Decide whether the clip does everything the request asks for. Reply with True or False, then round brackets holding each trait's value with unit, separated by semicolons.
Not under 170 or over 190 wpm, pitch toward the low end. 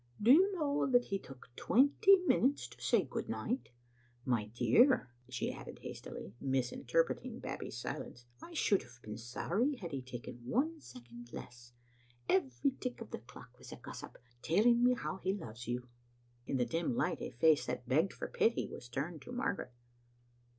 False (180 wpm; 155 Hz)